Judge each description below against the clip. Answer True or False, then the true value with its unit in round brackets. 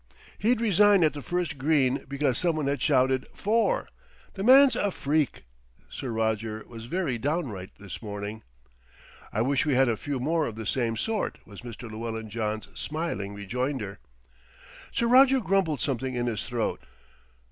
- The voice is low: True (130 Hz)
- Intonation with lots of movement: True (6.8 semitones)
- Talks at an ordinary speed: True (160 wpm)